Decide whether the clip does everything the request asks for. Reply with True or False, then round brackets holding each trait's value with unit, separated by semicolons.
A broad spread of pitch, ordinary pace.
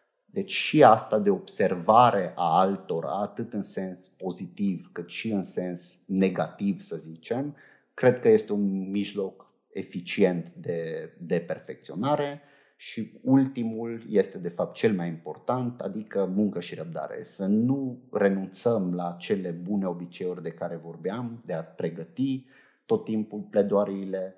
False (4.4 semitones; 135 wpm)